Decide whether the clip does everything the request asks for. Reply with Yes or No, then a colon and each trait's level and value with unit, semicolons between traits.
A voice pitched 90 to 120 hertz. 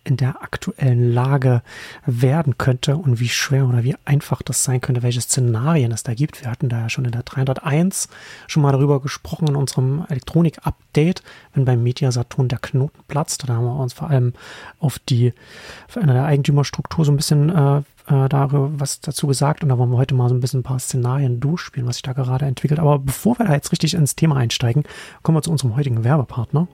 No: low, 135 Hz